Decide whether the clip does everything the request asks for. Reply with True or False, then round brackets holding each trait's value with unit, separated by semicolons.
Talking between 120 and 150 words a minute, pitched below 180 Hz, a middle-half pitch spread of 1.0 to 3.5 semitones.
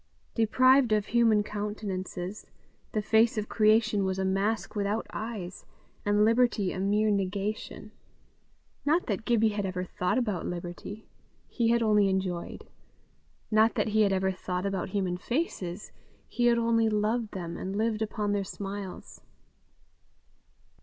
False (140 wpm; 210 Hz; 2.6 semitones)